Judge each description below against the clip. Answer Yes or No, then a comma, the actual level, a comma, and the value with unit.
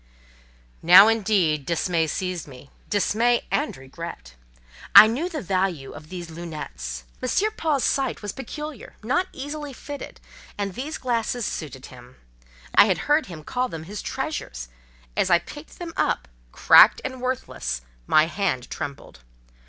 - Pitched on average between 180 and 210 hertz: Yes, high, 190 Hz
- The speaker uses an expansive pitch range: Yes, wide, 8.7 semitones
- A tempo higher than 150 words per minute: No, average, 140 wpm